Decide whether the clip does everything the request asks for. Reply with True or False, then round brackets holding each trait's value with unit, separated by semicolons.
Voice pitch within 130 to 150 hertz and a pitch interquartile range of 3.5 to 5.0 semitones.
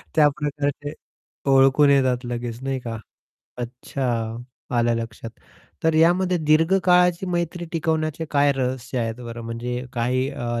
True (135 Hz; 4.7 semitones)